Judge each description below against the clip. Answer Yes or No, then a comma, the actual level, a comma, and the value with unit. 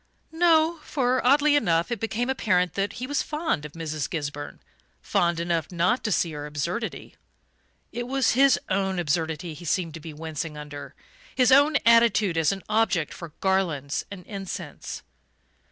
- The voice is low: No, medium, 185 Hz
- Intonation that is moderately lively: No, wide, 7.2 semitones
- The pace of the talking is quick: No, average, 160 wpm